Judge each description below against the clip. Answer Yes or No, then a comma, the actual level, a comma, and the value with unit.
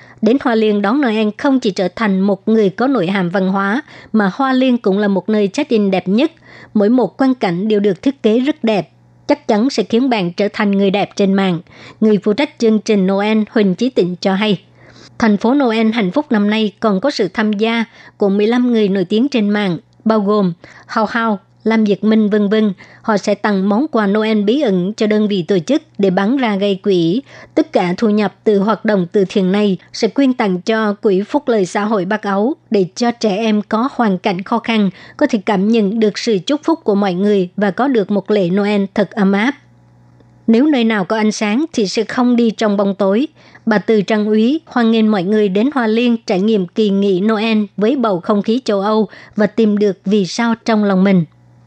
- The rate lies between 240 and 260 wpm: No, average, 230 wpm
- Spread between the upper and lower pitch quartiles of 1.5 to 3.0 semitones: Yes, narrow, 2.4 semitones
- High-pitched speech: Yes, high, 215 Hz